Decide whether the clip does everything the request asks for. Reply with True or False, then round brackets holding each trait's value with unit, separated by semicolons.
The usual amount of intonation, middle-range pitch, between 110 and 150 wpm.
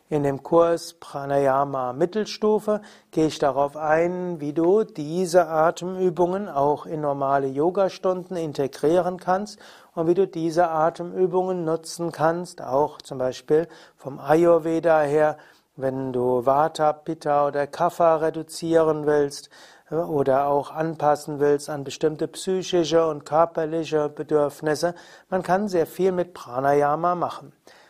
True (3.2 semitones; 160 Hz; 125 wpm)